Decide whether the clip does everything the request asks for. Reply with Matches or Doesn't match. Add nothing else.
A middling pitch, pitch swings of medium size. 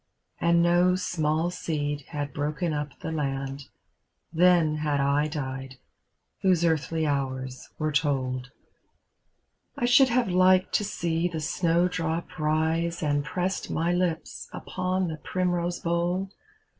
Matches